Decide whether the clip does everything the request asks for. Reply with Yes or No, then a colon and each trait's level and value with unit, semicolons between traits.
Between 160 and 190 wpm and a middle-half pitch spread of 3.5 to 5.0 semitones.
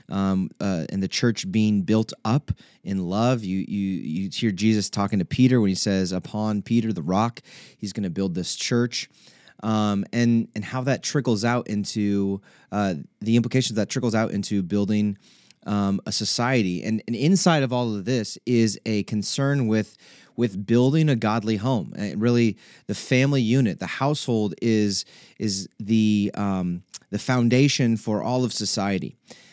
No: average, 170 wpm; average, 3.0 semitones